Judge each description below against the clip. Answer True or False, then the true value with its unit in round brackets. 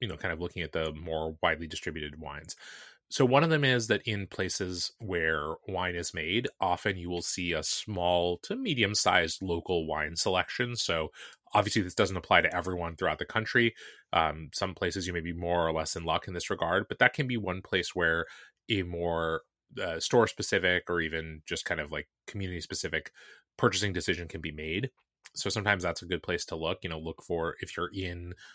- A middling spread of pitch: True (3.3 semitones)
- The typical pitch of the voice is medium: False (90 Hz)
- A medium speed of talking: False (210 wpm)